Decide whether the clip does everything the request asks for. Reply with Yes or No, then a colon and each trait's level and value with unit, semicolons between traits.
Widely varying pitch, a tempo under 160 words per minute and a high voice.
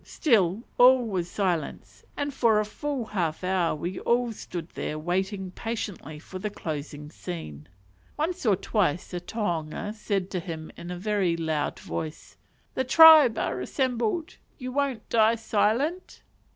Yes: wide, 5.7 semitones; average, 150 wpm; high, 200 Hz